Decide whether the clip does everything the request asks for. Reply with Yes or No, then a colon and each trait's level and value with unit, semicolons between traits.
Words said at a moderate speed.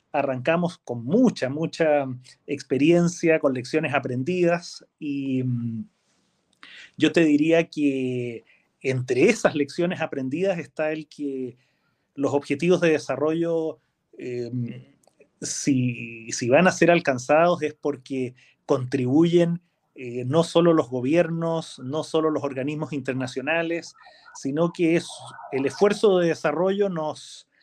No: slow, 115 wpm